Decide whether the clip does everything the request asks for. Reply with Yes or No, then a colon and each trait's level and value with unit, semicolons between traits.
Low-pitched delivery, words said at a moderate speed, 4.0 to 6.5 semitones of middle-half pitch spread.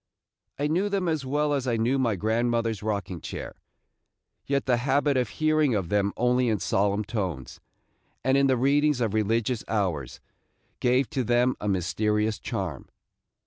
Yes: low, 120 Hz; average, 160 wpm; average, 4.5 semitones